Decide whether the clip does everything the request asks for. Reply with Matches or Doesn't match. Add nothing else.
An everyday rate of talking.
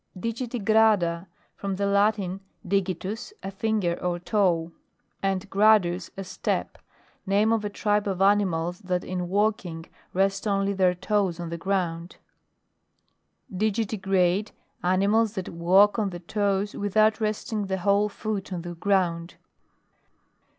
Doesn't match